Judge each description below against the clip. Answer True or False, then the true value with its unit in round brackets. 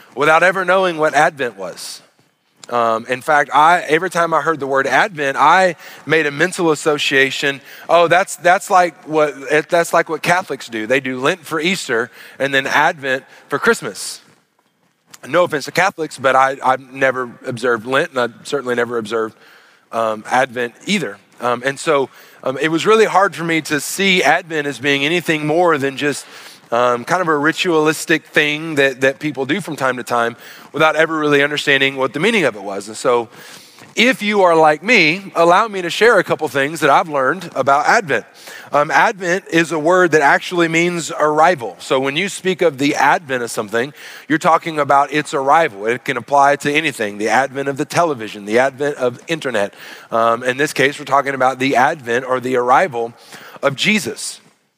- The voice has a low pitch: False (150 Hz)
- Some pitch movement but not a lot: True (4.0 semitones)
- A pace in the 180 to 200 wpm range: True (190 wpm)